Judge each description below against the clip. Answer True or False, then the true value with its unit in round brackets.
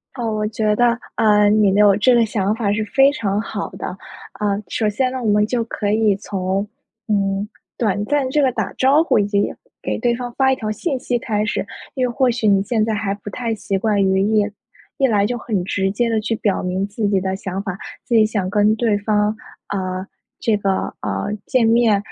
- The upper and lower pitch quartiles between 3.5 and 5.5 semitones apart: False (2.6 semitones)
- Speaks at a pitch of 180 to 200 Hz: False (210 Hz)